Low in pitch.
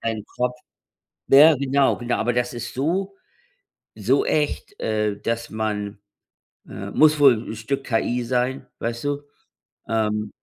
Yes: low, 120 Hz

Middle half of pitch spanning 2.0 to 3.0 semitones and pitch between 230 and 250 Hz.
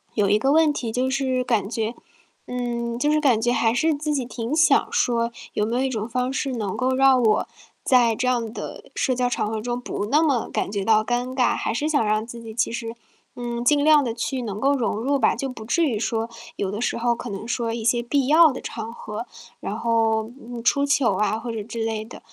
Yes: average, 2.7 semitones; high, 240 Hz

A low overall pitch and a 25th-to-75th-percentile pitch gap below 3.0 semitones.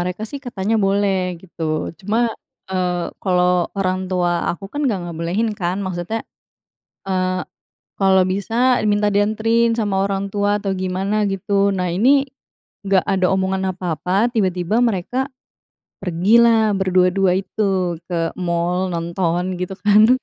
No: high, 190 Hz; narrow, 2.4 semitones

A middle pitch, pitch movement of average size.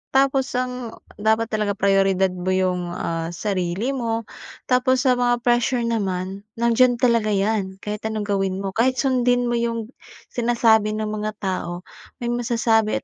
No: high, 220 Hz; average, 3.7 semitones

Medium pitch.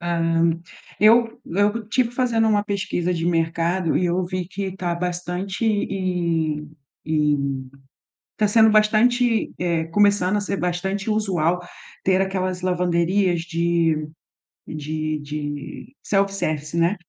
Yes: medium, 180 Hz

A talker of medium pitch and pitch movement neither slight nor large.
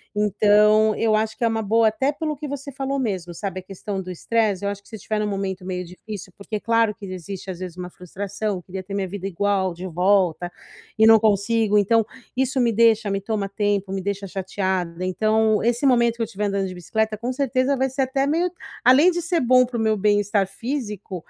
No: high, 210 Hz; average, 3.2 semitones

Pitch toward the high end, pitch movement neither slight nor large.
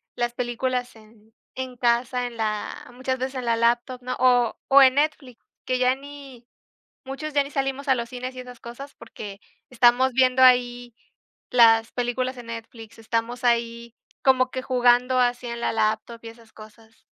No: high, 245 Hz; narrow, 1.7 semitones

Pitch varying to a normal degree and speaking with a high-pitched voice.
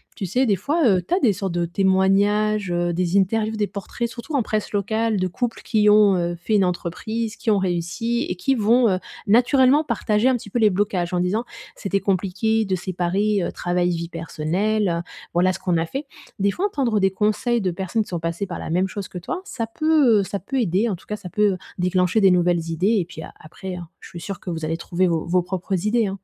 Yes: average, 3.5 semitones; high, 195 Hz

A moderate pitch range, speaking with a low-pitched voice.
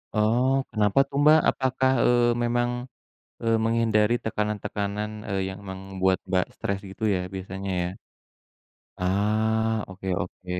Yes: average, 3.2 semitones; low, 105 Hz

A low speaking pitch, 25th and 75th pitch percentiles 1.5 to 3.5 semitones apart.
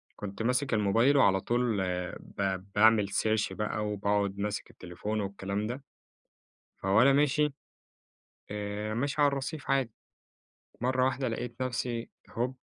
No: low, 110 Hz; average, 4.0 semitones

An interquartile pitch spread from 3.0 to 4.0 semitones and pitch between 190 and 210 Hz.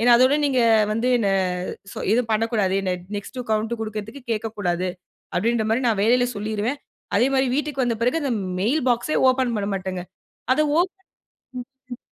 No: average, 3.3 semitones; high, 225 Hz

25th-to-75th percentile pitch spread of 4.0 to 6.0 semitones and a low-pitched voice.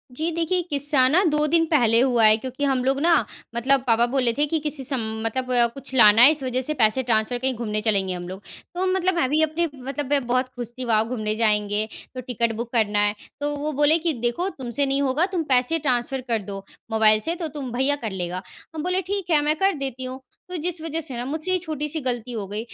No: average, 4.7 semitones; very high, 260 Hz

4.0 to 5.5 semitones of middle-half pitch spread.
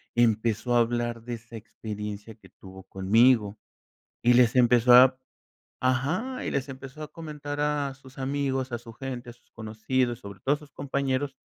No: average, 3.0 semitones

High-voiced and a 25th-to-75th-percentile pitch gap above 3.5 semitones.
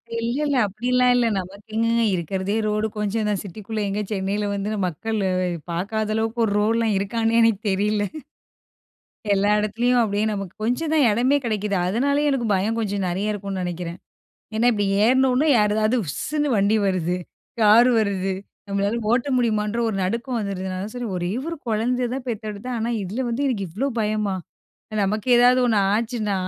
No: high, 215 Hz; average, 3.1 semitones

